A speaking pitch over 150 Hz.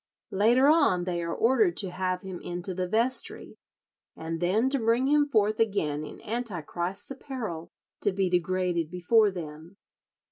Yes: high, 190 Hz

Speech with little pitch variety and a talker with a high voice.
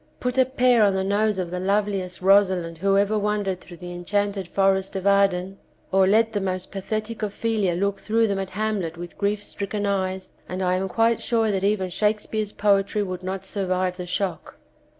Yes: narrow, 2.1 semitones; high, 195 Hz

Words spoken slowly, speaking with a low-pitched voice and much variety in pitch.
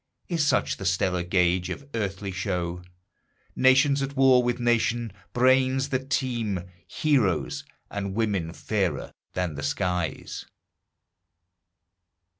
Yes: slow, 110 wpm; low, 105 Hz; wide, 6.3 semitones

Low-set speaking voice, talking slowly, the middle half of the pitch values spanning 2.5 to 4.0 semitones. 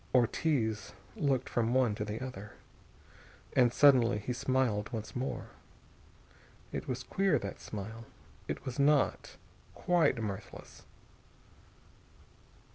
Yes: low, 120 Hz; slow, 110 wpm; average, 3.6 semitones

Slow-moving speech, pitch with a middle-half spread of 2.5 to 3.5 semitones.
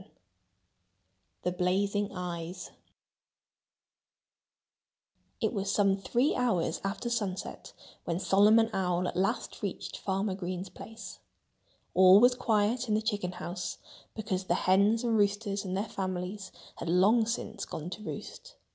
Yes: slow, 130 wpm; average, 3.1 semitones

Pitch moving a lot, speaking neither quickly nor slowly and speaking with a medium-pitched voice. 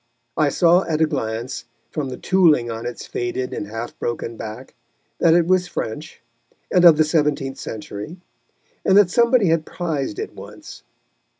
Yes: wide, 6.4 semitones; average, 165 wpm; medium, 150 Hz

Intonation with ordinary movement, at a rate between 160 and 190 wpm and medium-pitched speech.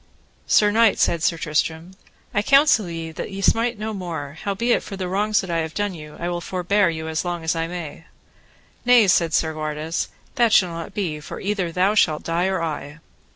No: average, 4.0 semitones; average, 200 wpm; medium, 175 Hz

